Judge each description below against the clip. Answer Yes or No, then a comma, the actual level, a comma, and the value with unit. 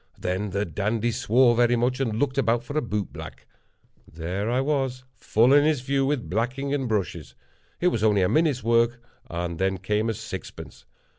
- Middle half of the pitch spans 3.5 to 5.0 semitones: Yes, average, 4.5 semitones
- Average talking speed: Yes, average, 190 wpm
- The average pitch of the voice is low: Yes, low, 115 Hz